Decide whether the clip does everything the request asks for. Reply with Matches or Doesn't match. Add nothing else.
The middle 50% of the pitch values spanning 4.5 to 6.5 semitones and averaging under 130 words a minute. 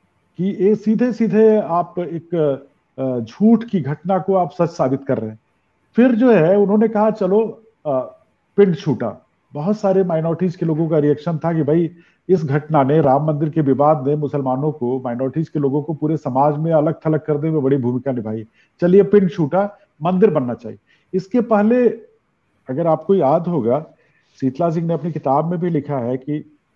Doesn't match